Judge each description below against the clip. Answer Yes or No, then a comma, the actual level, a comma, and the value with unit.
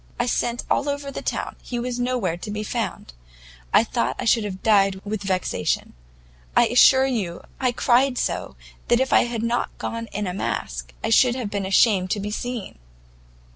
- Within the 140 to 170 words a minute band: No, average, 190 wpm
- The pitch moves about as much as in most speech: Yes, average, 3.8 semitones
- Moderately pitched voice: No, high, 225 Hz